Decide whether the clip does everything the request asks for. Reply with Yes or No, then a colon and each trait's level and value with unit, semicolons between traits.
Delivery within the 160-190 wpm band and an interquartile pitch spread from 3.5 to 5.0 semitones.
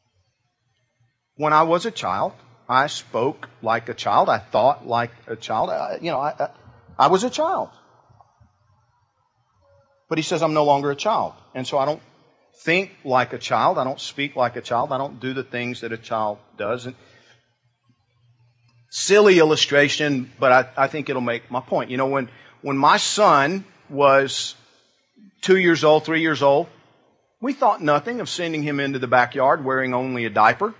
Yes: average, 180 wpm; average, 4.2 semitones